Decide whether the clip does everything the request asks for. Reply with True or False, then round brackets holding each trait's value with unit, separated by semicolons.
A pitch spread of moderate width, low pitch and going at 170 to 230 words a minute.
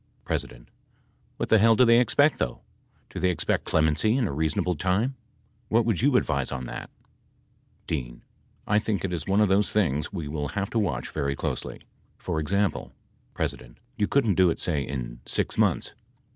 False (6.4 semitones; 95 Hz; 180 wpm)